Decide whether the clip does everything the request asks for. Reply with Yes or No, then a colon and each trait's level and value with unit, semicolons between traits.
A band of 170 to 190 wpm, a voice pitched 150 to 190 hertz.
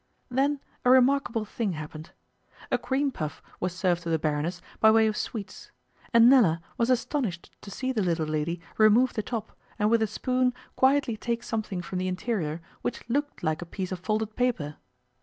No: average, 185 wpm; high, 215 Hz